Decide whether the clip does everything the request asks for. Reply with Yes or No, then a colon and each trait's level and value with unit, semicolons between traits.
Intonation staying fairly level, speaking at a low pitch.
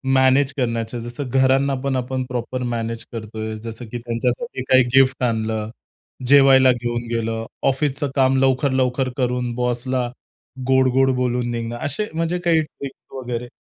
Yes: narrow, 2.1 semitones; low, 125 Hz